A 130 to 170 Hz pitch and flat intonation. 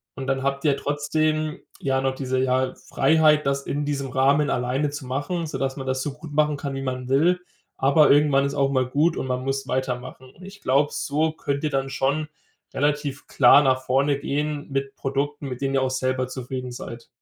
Yes: medium, 140 Hz; narrow, 1.9 semitones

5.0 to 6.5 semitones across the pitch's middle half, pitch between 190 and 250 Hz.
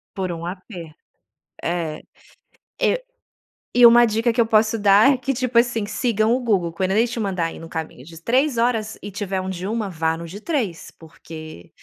Yes: wide, 5.5 semitones; high, 205 Hz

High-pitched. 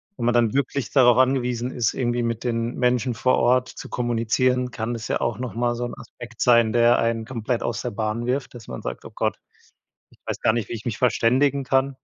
No: low, 120 Hz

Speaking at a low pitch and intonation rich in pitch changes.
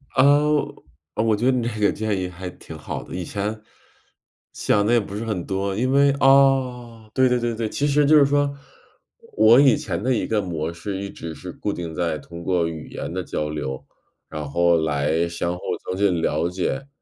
Yes: low, 100 Hz; wide, 6.5 semitones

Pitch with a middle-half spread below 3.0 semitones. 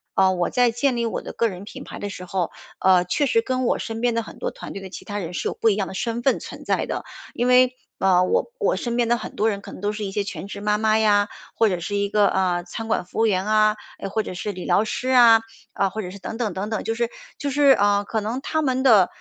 No: average, 3.4 semitones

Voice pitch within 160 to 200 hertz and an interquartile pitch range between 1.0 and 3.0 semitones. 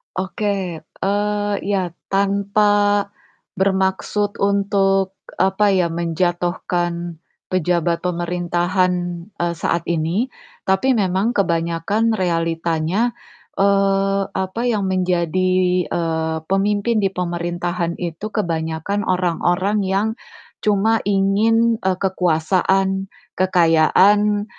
Yes: high, 190 Hz; average, 2.7 semitones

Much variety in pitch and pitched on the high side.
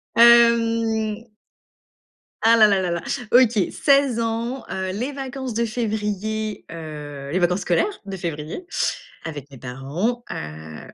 Yes: wide, 5.9 semitones; high, 215 Hz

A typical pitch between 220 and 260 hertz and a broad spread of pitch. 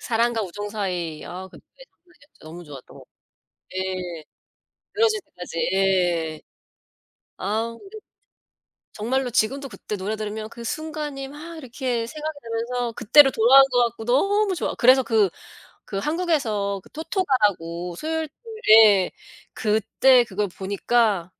Yes: high, 225 Hz; wide, 5.9 semitones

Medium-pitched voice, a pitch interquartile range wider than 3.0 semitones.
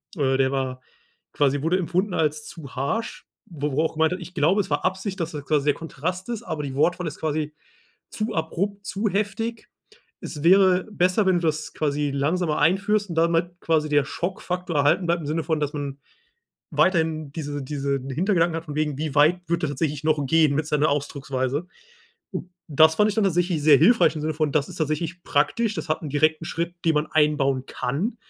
Yes: medium, 155 Hz; average, 3.7 semitones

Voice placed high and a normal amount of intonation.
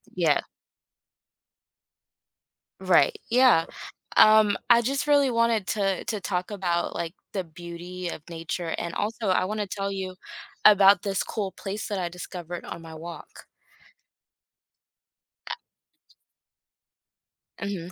Yes: high, 195 Hz; average, 3.5 semitones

